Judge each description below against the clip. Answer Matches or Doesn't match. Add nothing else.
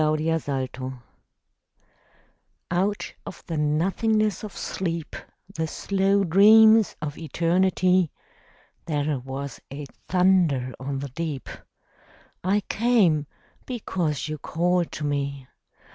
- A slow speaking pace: Matches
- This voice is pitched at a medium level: Matches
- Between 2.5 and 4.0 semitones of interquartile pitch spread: Doesn't match